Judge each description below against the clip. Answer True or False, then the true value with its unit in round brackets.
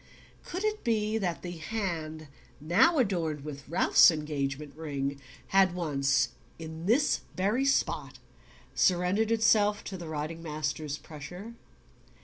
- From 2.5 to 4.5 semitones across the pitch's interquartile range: False (5.6 semitones)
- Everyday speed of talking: False (125 wpm)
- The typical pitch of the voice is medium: True (170 Hz)